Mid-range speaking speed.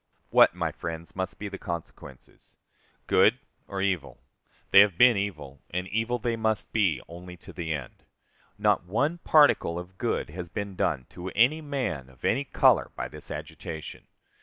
Yes: average, 165 wpm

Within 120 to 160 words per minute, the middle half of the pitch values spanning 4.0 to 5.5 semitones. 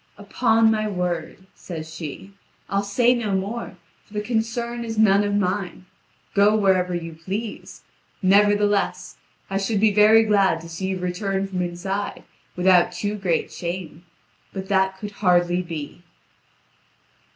No: average, 140 wpm; average, 2.7 semitones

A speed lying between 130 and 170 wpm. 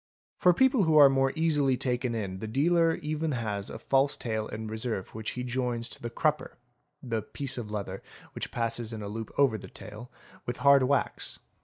No: fast, 205 wpm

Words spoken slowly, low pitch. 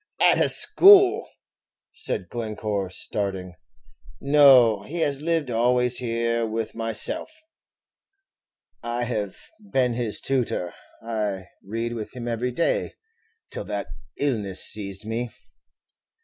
Yes: slow, 110 wpm; low, 115 Hz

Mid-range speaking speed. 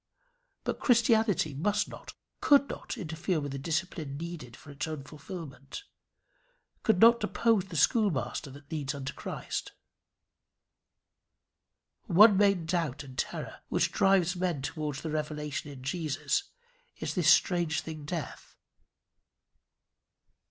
No: slow, 125 wpm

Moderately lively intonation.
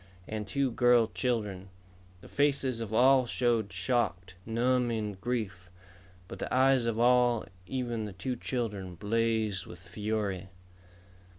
Yes: average, 3.4 semitones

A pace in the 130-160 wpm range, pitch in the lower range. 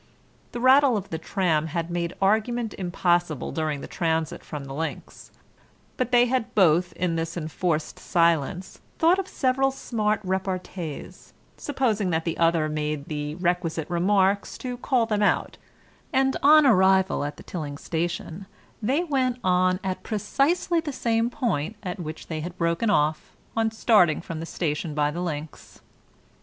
No: average, 155 wpm; medium, 180 Hz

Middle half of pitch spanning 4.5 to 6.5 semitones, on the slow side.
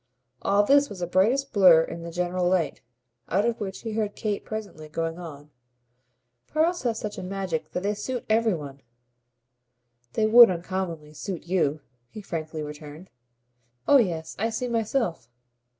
No: average, 5.0 semitones; average, 160 wpm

